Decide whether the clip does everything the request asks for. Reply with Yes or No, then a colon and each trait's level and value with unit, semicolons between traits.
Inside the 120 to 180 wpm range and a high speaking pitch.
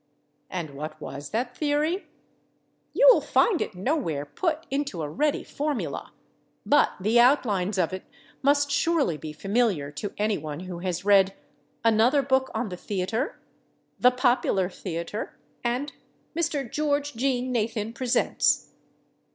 Yes: slow, 135 wpm; high, 230 Hz